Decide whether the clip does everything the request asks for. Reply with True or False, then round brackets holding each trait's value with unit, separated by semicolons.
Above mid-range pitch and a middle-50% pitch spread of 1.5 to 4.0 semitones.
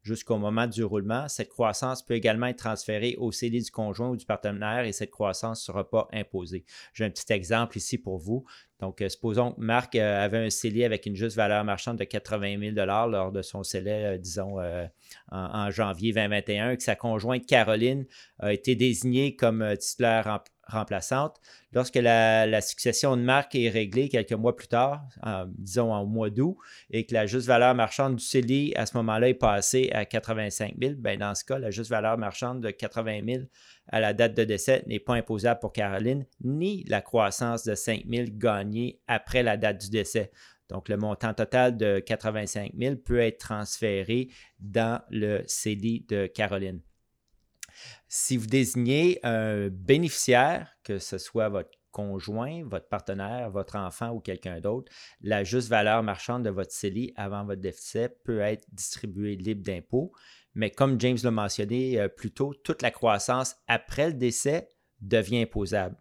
False (110 Hz; 2.9 semitones)